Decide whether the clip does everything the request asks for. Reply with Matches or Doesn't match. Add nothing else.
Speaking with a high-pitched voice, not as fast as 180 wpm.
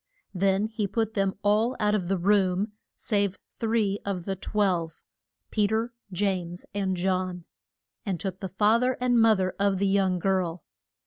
Matches